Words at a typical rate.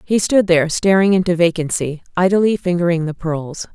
Yes: average, 160 wpm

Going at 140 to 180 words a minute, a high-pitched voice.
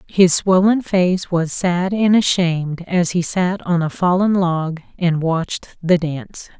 No: average, 165 wpm; medium, 175 Hz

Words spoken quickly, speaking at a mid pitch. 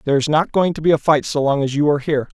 Yes: fast, 325 wpm; medium, 150 Hz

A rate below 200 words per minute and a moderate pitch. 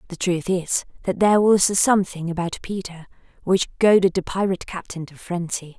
Yes: average, 175 wpm; medium, 180 Hz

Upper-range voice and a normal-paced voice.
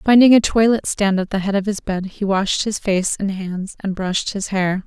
No: high, 200 Hz; fast, 245 wpm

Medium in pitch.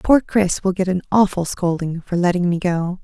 Yes: medium, 180 Hz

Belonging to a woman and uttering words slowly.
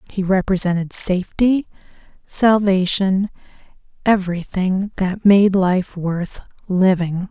Yes: female; slow, 80 wpm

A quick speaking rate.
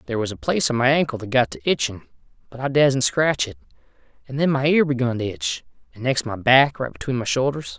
Yes: fast, 240 wpm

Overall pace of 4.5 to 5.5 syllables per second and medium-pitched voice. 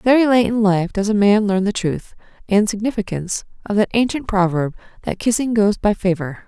No: 4.8 syllables/s; high, 205 Hz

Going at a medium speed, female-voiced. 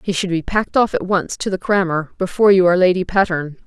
No: fast, 245 wpm; female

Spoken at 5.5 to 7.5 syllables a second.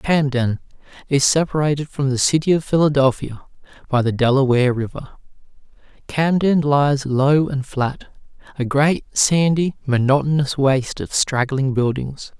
No: 4.5 syllables/s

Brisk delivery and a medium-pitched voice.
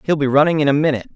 Yes: fast, 310 wpm; medium, 145 Hz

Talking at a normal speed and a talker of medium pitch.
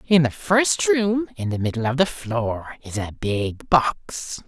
Yes: average, 190 wpm; medium, 145 Hz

